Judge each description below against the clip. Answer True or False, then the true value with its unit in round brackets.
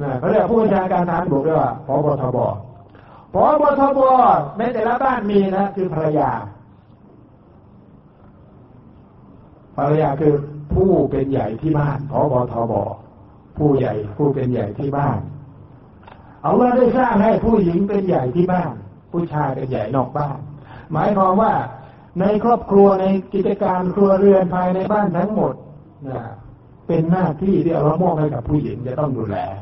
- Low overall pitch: False (150 Hz)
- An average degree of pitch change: False (7.1 semitones)